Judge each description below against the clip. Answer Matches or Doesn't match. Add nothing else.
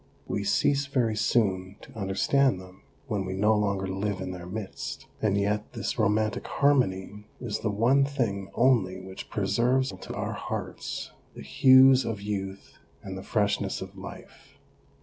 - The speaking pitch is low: Matches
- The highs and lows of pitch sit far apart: Doesn't match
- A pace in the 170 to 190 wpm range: Doesn't match